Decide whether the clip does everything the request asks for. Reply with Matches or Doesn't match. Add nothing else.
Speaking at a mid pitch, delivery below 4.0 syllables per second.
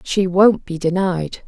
Matches